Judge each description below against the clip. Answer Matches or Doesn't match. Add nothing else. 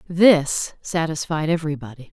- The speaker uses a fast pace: Doesn't match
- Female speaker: Matches